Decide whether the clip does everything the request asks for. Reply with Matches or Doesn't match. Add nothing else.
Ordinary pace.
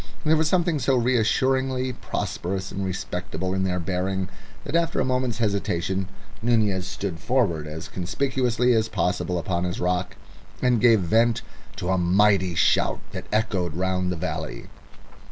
Matches